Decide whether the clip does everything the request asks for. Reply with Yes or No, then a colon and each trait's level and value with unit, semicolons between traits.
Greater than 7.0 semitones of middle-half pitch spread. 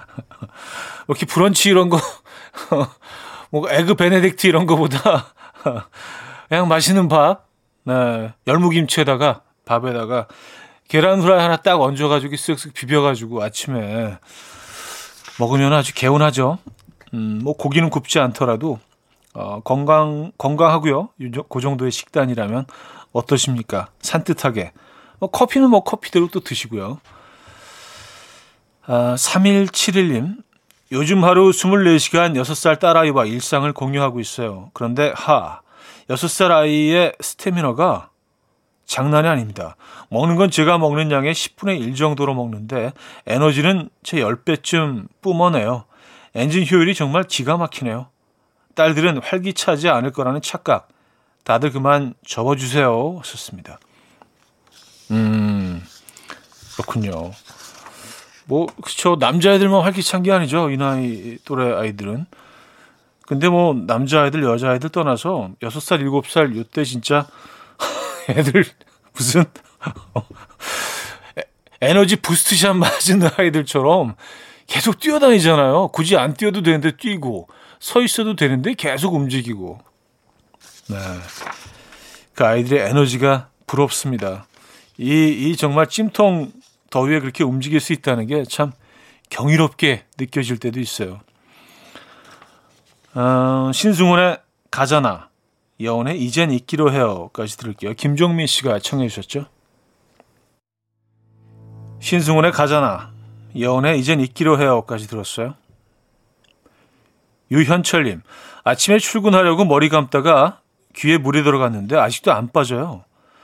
No: wide, 5.5 semitones